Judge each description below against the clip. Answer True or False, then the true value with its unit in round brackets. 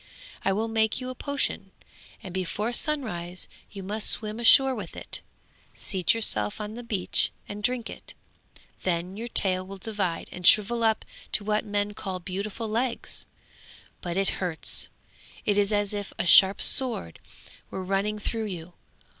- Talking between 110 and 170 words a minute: True (160 wpm)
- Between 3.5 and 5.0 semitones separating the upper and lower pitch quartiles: False (3.1 semitones)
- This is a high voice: True (205 Hz)